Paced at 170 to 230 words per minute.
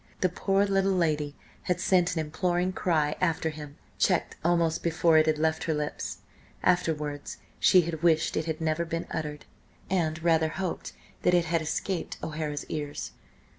No: average, 160 wpm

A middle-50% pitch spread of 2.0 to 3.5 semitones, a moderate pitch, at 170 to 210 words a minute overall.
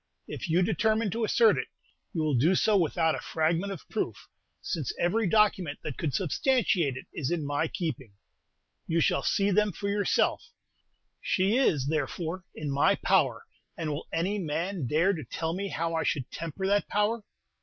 No: average, 4.5 semitones; medium, 170 Hz; average, 175 wpm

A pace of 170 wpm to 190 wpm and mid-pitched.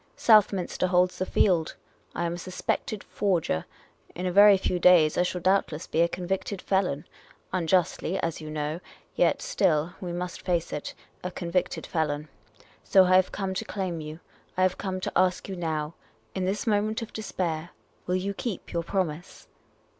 Yes: average, 180 wpm; medium, 180 Hz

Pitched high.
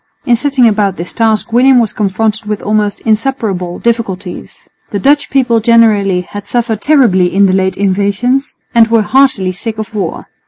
Yes: high, 215 Hz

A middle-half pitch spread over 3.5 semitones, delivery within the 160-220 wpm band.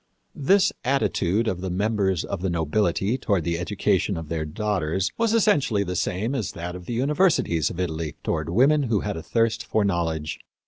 Yes: average, 5.1 semitones; average, 190 wpm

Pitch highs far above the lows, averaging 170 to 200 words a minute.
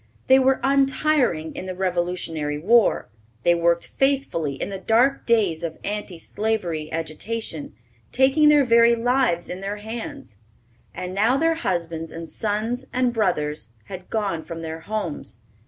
No: wide, 6.4 semitones; average, 145 wpm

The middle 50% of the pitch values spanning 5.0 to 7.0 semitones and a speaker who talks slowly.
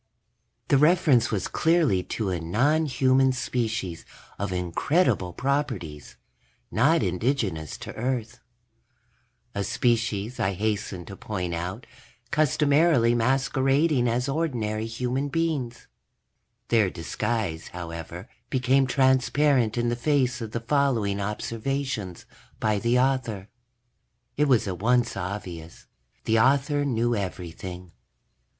Yes: wide, 5.4 semitones; slow, 110 wpm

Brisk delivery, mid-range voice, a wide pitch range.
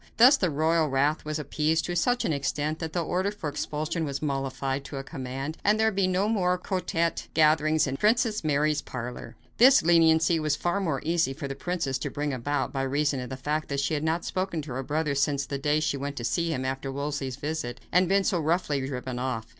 No: fast, 225 wpm; medium, 150 Hz; average, 3.6 semitones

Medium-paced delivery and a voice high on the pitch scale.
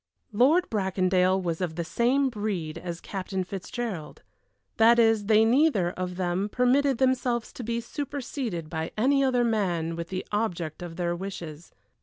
Yes: average, 155 wpm; high, 200 Hz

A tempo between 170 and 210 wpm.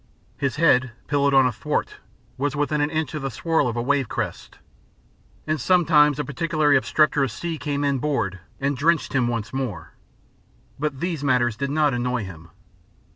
Yes: average, 175 wpm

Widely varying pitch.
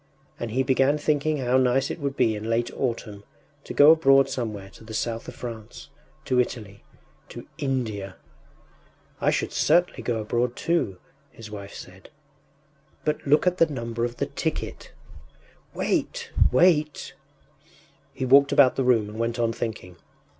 No: average, 3.7 semitones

